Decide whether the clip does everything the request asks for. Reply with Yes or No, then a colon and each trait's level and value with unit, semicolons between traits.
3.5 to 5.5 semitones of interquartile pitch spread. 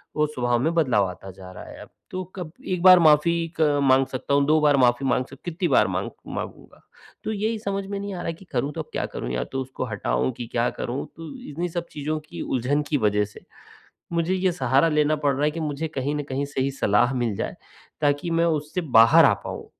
Yes: average, 4.7 semitones